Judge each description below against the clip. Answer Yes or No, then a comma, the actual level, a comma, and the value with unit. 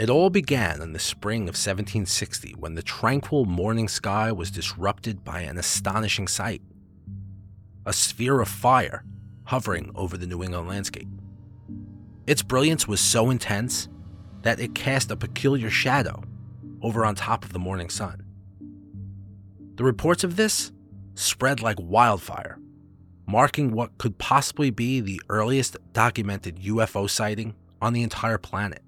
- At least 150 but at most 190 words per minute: No, average, 140 wpm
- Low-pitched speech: Yes, low, 105 Hz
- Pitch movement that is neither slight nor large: Yes, average, 3.1 semitones